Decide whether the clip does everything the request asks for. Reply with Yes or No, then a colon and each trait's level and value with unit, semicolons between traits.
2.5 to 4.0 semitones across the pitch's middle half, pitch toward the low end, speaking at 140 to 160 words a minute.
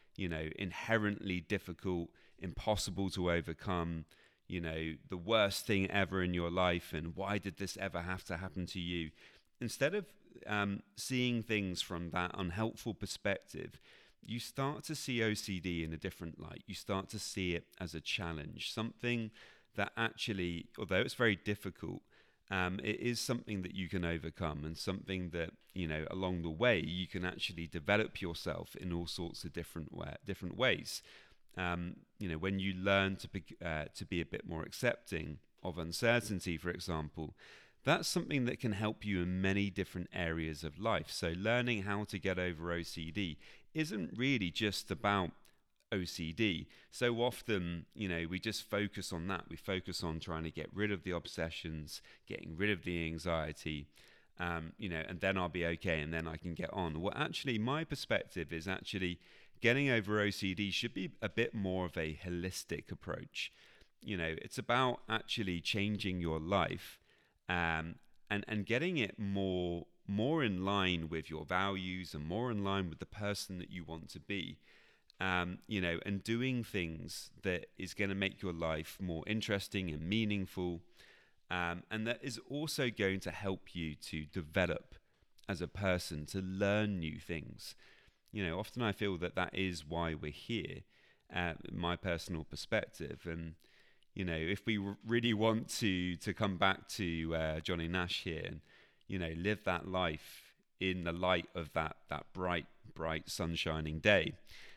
No: average, 3.5 semitones; very low, 95 Hz; average, 170 wpm